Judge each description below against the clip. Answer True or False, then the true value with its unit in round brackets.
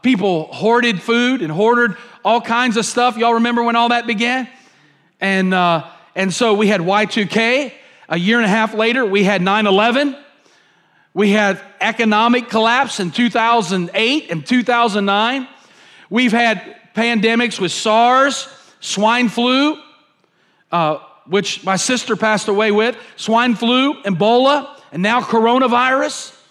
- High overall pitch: True (230 Hz)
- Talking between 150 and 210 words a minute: False (135 wpm)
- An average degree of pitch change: True (3.4 semitones)